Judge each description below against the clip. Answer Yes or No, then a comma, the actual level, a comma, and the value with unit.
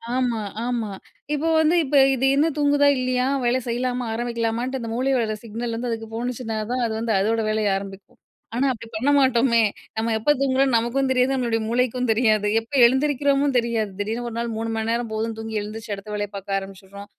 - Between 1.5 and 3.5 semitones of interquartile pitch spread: Yes, narrow, 2.5 semitones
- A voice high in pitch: Yes, high, 235 Hz